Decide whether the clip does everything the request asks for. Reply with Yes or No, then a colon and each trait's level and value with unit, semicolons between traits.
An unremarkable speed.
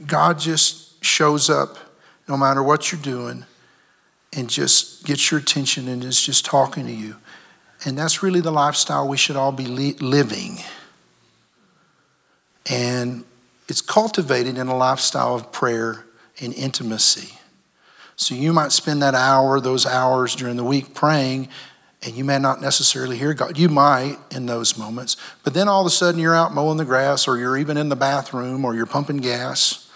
Yes: average, 170 wpm